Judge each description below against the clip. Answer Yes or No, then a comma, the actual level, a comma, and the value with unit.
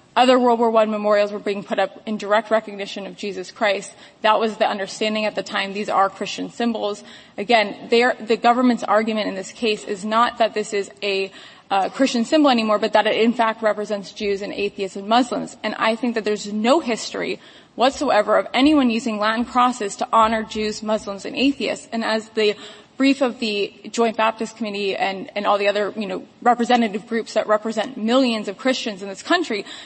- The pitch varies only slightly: Yes, narrow, 2.3 semitones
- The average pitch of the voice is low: No, high, 220 Hz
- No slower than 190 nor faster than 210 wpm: Yes, average, 200 wpm